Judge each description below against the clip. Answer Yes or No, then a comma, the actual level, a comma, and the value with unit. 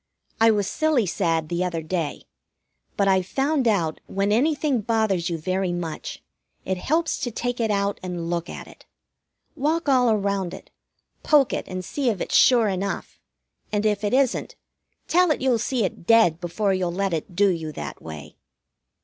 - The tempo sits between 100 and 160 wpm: No, average, 180 wpm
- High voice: Yes, high, 200 Hz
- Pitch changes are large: Yes, wide, 5.7 semitones